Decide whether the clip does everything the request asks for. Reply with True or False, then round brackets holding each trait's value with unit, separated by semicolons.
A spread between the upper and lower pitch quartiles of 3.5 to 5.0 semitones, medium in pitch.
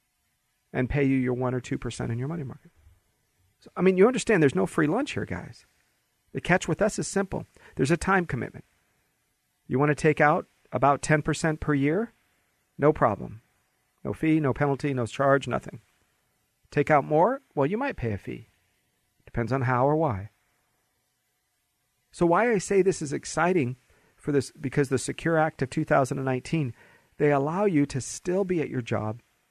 True (4.3 semitones; 145 Hz)